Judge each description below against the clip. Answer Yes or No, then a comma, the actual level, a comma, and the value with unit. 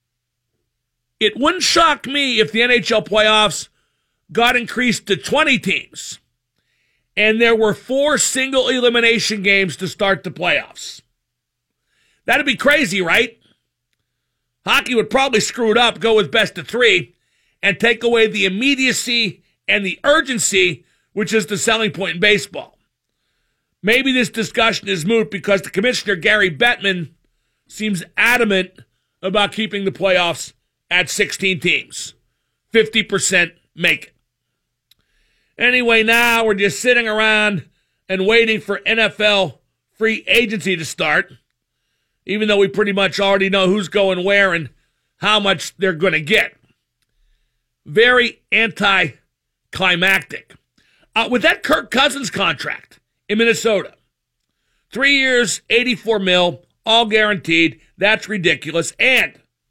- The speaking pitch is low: No, high, 210 Hz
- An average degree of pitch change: Yes, average, 3.6 semitones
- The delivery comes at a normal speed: No, slow, 125 wpm